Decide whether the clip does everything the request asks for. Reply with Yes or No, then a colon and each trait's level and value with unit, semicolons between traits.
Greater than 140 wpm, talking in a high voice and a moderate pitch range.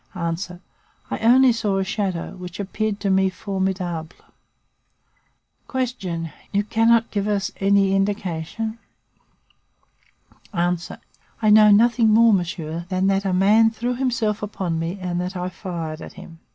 No: slow, 135 wpm; high, 195 Hz; average, 3.3 semitones